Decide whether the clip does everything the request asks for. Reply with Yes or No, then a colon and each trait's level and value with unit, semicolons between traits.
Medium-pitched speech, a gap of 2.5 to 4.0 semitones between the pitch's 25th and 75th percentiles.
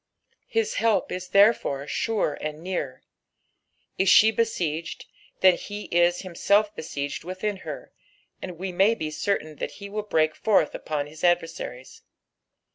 No: medium, 180 Hz; average, 4.9 semitones